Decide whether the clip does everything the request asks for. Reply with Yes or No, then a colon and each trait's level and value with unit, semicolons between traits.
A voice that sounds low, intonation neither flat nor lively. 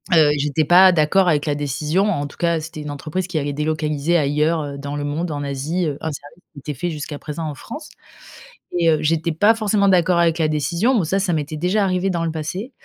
No: medium, 160 Hz; average, 3.2 semitones